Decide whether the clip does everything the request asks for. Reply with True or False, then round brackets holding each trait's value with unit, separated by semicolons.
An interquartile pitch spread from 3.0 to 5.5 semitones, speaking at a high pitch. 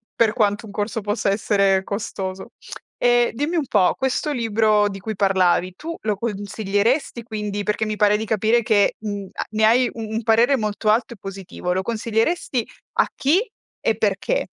False (2.5 semitones; 215 Hz)